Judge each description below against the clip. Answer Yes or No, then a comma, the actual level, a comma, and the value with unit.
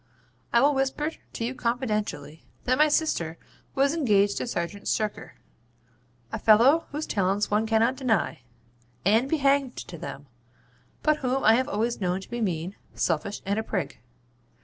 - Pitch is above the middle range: Yes, high, 225 Hz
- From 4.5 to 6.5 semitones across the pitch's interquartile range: Yes, average, 5.1 semitones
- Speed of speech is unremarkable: Yes, average, 160 wpm